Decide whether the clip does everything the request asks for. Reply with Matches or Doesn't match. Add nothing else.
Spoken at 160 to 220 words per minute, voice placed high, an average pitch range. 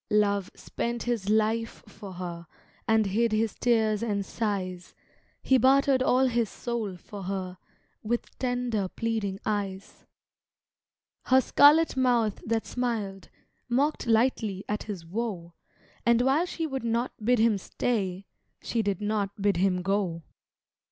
Doesn't match